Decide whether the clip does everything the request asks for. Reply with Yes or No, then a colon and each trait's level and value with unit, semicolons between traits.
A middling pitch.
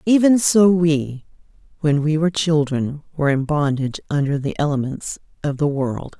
Yes: medium, 150 Hz